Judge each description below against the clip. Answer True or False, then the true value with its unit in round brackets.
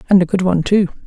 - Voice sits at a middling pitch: True (180 Hz)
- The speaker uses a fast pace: True (280 wpm)